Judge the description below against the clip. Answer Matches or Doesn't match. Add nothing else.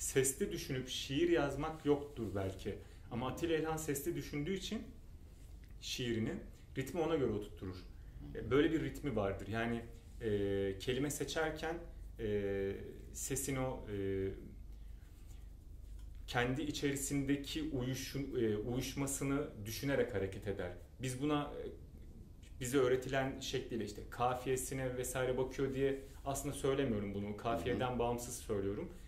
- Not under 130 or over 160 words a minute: Doesn't match